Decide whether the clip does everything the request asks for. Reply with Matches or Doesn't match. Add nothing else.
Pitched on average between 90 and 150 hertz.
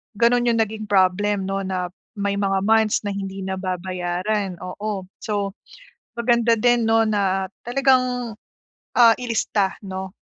Doesn't match